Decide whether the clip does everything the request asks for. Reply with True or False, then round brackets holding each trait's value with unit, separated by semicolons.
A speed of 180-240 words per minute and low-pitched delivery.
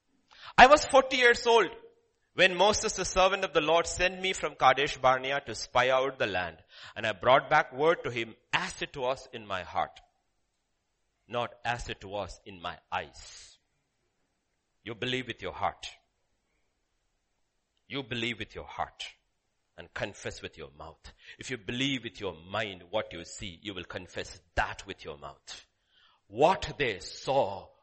False (165 wpm; 125 Hz)